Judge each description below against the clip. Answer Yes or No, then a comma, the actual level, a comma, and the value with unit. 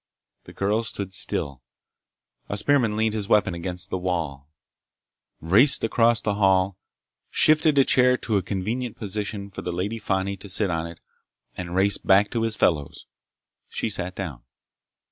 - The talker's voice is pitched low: Yes, low, 100 Hz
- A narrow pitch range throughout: No, average, 3.5 semitones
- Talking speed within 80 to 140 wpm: No, average, 160 wpm